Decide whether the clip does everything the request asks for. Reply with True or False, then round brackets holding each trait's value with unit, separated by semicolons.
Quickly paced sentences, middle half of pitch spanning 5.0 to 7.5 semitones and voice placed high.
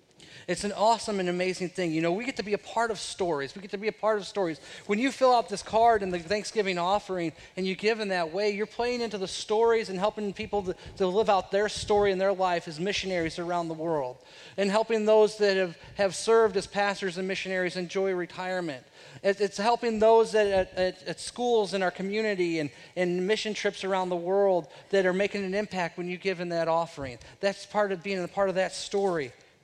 False (230 wpm; 2.7 semitones; 195 Hz)